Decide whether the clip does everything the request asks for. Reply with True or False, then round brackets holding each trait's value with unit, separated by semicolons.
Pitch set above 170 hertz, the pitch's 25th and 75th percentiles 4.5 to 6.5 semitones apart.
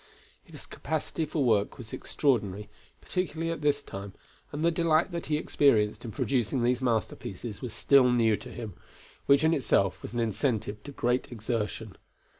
False (125 Hz; 5.2 semitones)